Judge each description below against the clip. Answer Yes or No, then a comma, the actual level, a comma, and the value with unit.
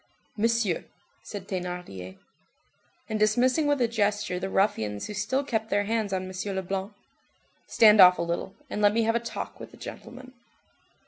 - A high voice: Yes, high, 205 Hz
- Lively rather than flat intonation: No, average, 3.5 semitones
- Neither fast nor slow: Yes, average, 170 wpm